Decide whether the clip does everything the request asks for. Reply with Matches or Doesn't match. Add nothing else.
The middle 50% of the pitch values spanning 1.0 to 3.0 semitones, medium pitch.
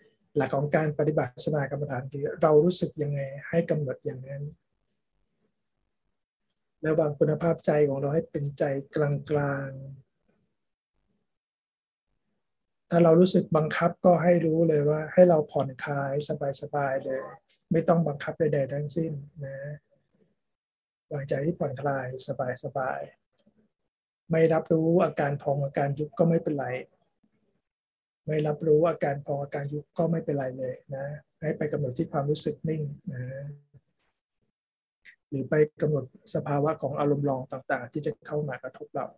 Matches